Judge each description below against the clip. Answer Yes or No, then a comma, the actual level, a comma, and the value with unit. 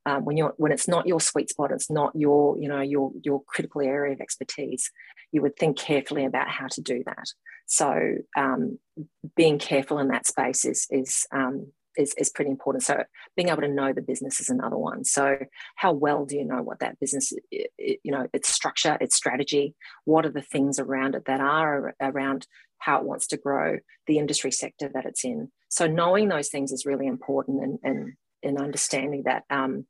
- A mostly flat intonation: Yes, narrow, 2.2 semitones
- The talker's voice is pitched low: No, medium, 145 Hz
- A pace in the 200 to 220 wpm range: Yes, fast, 205 wpm